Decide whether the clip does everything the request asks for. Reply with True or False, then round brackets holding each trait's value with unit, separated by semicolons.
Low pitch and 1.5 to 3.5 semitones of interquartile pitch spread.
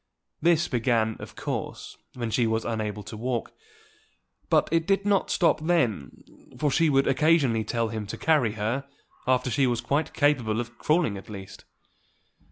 False (125 Hz; 5.5 semitones)